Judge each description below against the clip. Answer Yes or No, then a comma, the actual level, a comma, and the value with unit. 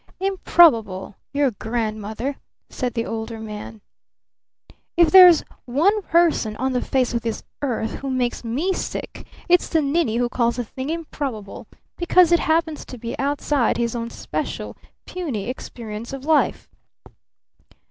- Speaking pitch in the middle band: No, very high, 255 Hz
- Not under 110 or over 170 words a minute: Yes, average, 140 wpm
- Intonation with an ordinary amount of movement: No, wide, 5.8 semitones